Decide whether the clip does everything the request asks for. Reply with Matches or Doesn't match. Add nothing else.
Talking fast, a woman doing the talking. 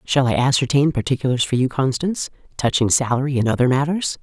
Doesn't match